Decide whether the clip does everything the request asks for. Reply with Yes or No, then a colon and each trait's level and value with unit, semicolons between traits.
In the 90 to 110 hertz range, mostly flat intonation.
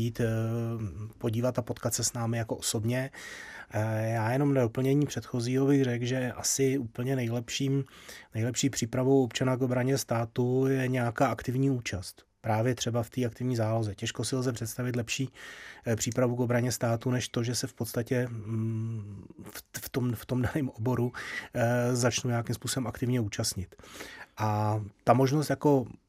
No: low, 120 Hz; narrow, 2.1 semitones